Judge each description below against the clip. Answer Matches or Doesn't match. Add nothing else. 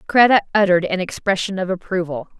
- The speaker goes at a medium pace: Matches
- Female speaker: Matches